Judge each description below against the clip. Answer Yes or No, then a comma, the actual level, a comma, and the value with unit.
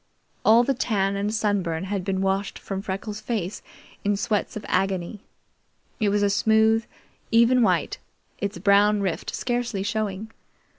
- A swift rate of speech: No, average, 145 wpm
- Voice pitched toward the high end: Yes, high, 205 Hz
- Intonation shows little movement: Yes, narrow, 2.2 semitones